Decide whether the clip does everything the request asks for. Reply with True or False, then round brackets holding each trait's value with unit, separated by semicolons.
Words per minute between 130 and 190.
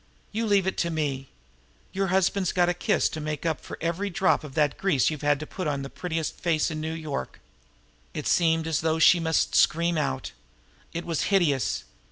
False (205 wpm)